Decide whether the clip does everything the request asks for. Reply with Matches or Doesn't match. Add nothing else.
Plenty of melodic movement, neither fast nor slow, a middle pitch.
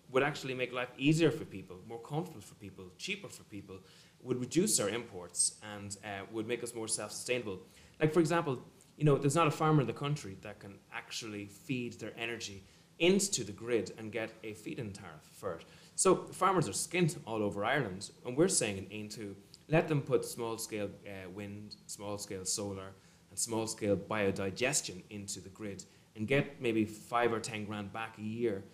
Doesn't match